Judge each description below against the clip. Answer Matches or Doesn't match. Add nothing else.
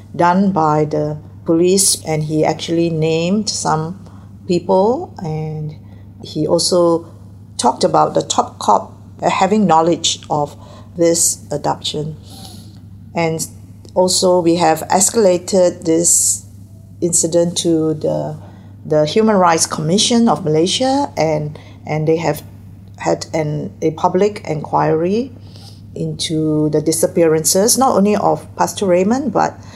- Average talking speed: Doesn't match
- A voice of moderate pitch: Matches